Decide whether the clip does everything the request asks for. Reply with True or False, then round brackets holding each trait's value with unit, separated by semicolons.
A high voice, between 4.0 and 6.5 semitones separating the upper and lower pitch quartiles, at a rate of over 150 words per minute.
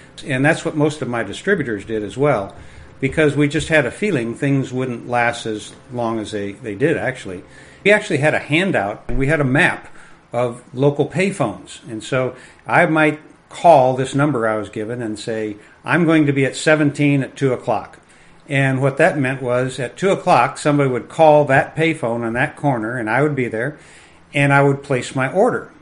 False (135 Hz; 4.3 semitones; 200 wpm)